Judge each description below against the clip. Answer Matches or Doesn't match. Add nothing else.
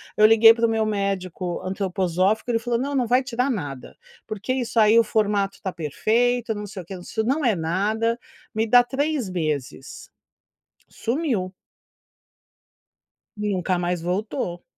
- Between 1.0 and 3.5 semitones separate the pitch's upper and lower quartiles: Doesn't match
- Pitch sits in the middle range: Doesn't match